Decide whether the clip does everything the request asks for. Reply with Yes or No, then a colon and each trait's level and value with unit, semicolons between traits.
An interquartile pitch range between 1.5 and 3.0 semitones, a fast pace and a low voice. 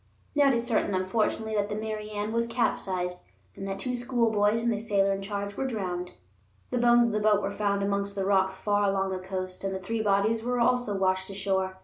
No: average, 2.7 semitones; fast, 225 wpm; high, 205 Hz